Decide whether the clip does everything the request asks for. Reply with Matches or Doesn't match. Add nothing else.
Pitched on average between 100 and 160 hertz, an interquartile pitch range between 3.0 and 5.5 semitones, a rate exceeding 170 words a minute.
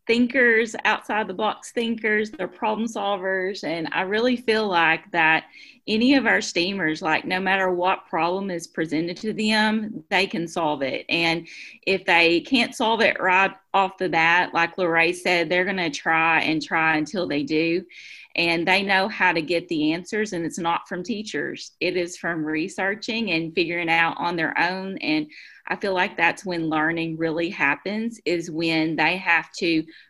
Doesn't match